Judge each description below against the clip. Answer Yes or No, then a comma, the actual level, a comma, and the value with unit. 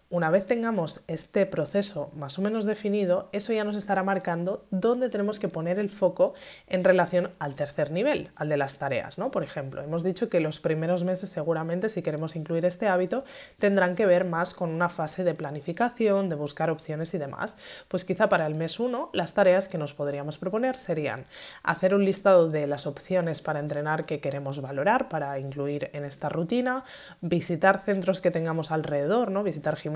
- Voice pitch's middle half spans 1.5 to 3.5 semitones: No, average, 4.2 semitones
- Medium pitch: Yes, medium, 175 Hz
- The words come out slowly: No, fast, 190 wpm